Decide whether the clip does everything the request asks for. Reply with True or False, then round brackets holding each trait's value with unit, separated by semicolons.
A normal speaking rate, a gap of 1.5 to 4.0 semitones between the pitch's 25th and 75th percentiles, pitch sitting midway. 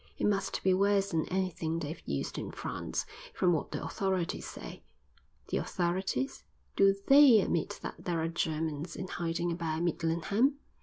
True (155 wpm; 2.8 semitones; 175 Hz)